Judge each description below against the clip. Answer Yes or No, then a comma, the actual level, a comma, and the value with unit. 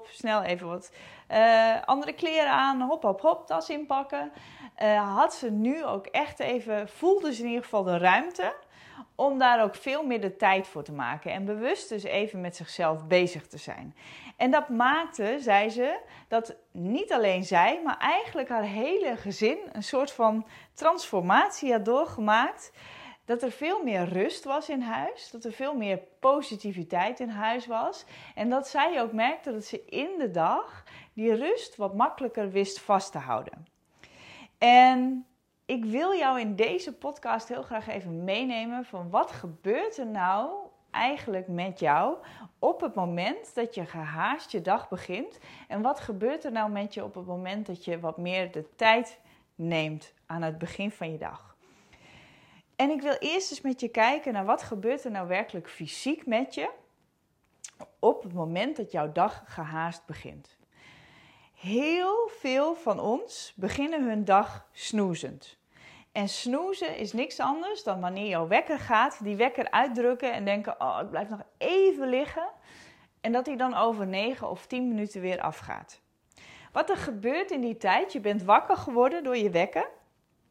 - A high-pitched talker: Yes, high, 225 Hz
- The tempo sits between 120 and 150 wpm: No, average, 170 wpm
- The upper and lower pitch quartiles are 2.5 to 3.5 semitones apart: No, wide, 5.6 semitones